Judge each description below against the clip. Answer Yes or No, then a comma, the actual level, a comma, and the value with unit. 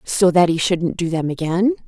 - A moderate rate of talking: No, fast, 225 wpm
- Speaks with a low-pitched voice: No, medium, 180 Hz